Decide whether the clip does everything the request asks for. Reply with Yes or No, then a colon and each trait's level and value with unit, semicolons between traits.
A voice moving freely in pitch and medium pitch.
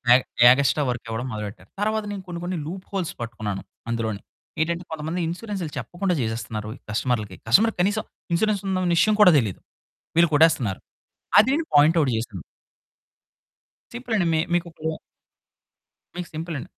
Yes: wide, 8.0 semitones; medium, 160 Hz